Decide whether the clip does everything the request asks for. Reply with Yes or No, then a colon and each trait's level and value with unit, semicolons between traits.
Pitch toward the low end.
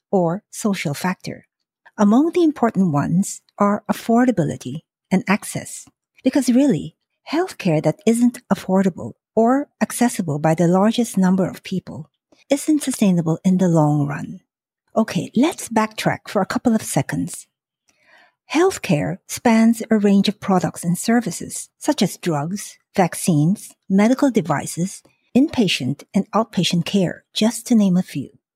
No: high, 205 Hz